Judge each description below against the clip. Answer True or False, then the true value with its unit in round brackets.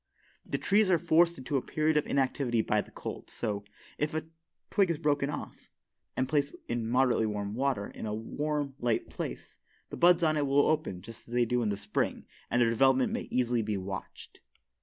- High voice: False (130 Hz)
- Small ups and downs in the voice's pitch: False (4.9 semitones)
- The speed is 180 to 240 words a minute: True (200 wpm)